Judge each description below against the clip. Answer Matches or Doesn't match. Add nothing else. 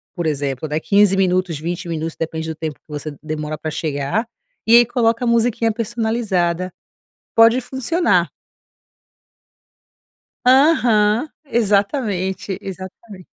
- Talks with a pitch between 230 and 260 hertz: Doesn't match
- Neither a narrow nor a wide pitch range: Doesn't match